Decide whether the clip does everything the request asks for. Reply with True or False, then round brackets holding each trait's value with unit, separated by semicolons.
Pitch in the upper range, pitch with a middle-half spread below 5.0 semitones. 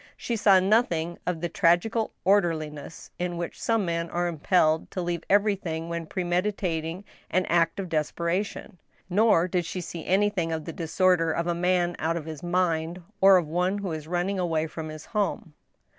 False (175 Hz; 2.4 semitones)